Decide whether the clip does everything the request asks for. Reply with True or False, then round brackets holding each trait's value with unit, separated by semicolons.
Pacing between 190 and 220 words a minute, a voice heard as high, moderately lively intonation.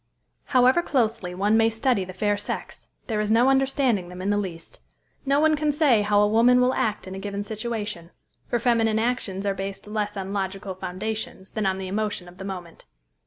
True (205 wpm; 210 Hz; 3.5 semitones)